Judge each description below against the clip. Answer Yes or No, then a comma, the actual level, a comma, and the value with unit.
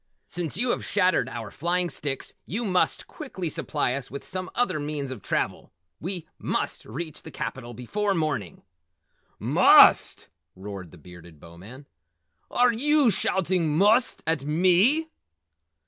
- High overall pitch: No, medium, 160 Hz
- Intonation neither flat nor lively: No, wide, 7.2 semitones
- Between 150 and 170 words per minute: No, slow, 135 wpm